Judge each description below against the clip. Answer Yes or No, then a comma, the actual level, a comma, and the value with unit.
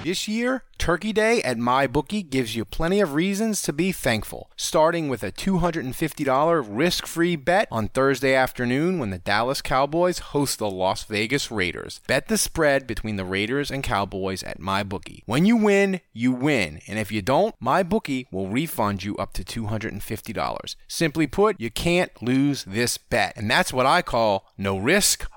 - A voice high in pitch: No, low, 135 Hz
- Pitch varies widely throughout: Yes, wide, 8.0 semitones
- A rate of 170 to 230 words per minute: Yes, average, 175 wpm